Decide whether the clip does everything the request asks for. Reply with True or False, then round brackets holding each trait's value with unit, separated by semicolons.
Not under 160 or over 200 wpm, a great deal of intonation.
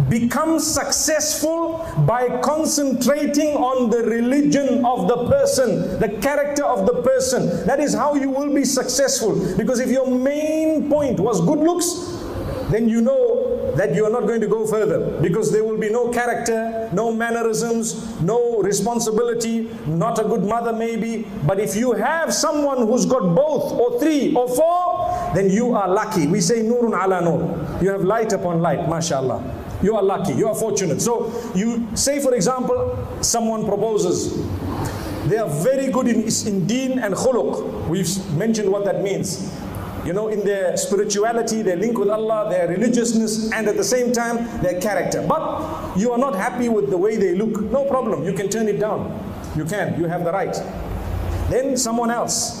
False (175 wpm; 4.6 semitones)